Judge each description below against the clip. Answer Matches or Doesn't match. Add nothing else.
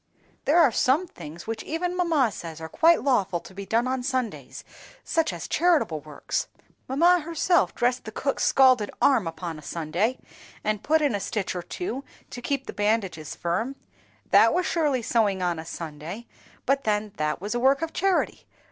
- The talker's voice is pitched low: Doesn't match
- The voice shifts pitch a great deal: Matches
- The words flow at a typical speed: Matches